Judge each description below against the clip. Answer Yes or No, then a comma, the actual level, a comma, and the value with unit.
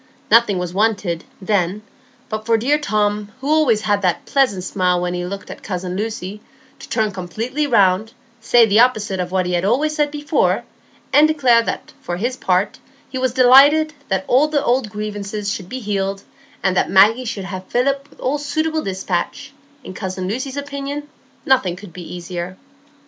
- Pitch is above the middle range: Yes, high, 215 Hz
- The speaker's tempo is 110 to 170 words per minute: No, average, 180 wpm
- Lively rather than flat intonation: Yes, wide, 5.7 semitones